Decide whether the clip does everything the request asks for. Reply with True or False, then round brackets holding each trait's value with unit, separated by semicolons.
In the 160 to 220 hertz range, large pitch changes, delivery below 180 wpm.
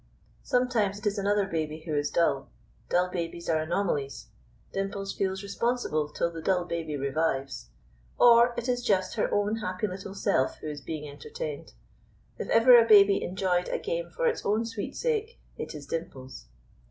True (190 Hz; 6.2 semitones; 170 wpm)